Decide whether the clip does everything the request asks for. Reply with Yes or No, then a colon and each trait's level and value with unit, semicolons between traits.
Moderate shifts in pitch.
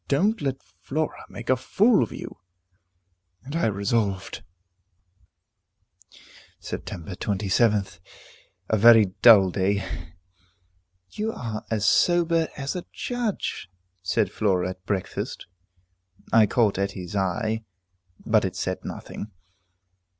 No: wide, 6.0 semitones